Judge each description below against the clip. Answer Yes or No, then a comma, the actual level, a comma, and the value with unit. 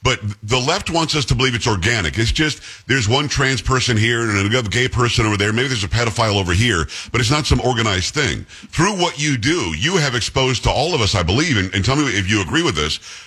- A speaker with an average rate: No, fast, 255 wpm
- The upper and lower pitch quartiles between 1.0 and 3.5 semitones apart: No, average, 3.9 semitones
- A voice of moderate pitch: No, low, 120 Hz